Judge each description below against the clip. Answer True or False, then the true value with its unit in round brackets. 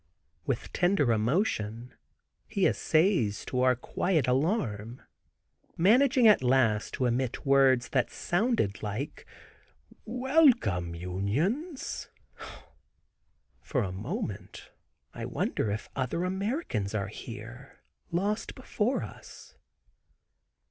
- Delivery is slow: True (95 wpm)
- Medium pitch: False (130 Hz)